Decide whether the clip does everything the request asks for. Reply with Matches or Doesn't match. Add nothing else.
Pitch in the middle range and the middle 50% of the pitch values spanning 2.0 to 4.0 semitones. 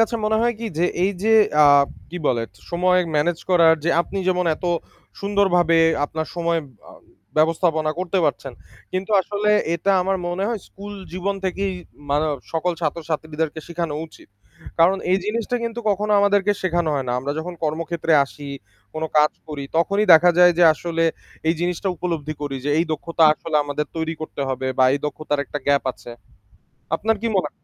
Matches